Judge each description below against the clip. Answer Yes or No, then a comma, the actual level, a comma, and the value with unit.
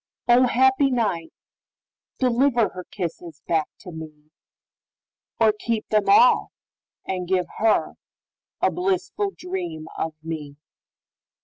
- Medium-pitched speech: No, high, 195 Hz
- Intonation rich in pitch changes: Yes, wide, 6.9 semitones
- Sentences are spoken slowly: Yes, slow, 95 wpm